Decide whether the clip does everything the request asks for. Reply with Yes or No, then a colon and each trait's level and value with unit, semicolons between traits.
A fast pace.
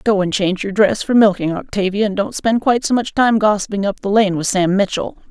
Yes: fast, 250 wpm